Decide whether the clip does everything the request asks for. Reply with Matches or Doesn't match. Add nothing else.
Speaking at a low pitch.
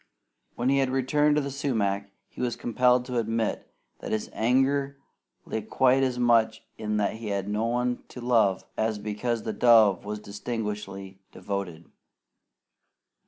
Matches